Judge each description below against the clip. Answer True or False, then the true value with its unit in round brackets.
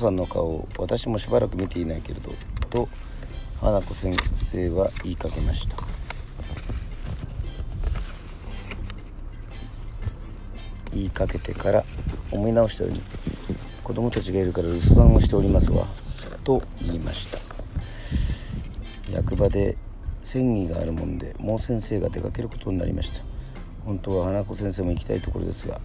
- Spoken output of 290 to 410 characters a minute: False (280 characters per minute)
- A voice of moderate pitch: False (95 Hz)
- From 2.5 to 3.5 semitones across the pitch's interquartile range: True (3.1 semitones)